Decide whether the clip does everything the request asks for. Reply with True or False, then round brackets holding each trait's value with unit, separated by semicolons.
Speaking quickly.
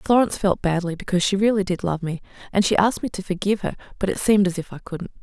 True (265 wpm)